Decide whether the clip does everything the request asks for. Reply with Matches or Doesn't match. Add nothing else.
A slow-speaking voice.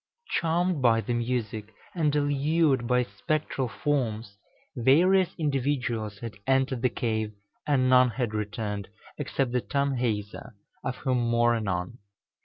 Matches